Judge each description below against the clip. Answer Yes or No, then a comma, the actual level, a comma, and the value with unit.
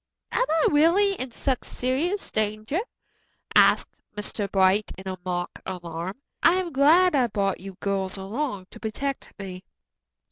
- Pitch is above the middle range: Yes, high, 215 Hz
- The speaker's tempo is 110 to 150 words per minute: Yes, average, 140 wpm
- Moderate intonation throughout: No, wide, 7.6 semitones